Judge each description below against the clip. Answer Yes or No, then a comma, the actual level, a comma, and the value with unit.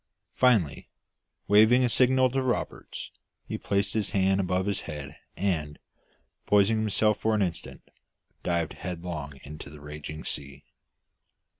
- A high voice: No, very low, 95 Hz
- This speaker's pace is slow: Yes, slow, 130 wpm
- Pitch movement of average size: No, wide, 6.1 semitones